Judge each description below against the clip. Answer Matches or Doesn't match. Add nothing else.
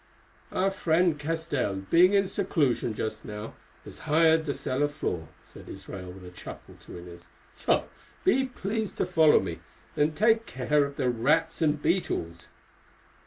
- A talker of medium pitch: Matches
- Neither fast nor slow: Matches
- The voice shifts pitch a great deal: Matches